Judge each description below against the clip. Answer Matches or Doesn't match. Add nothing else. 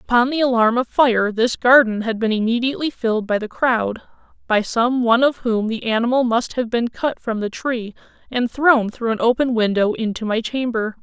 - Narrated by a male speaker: Doesn't match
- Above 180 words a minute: Matches